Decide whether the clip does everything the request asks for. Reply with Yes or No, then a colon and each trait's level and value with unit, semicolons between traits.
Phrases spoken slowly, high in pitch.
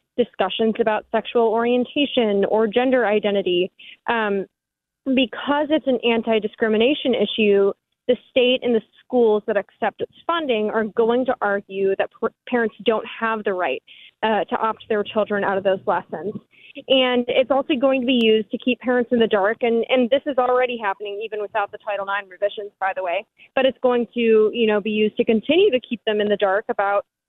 No: average, 190 wpm; high, 225 Hz